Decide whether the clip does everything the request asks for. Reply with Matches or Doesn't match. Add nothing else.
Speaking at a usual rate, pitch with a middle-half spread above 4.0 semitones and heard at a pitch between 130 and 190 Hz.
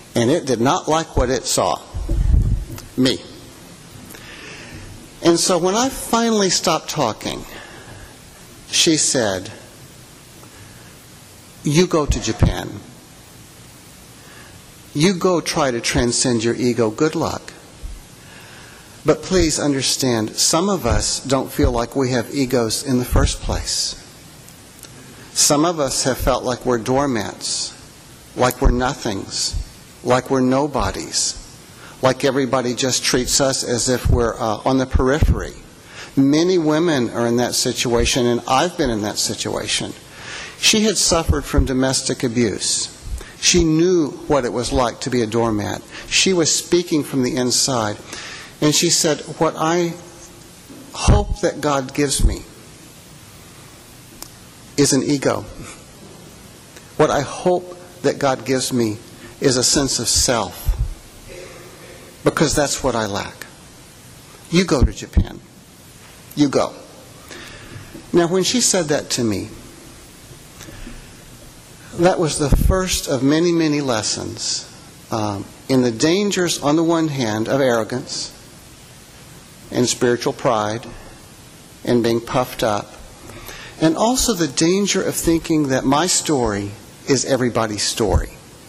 Doesn't match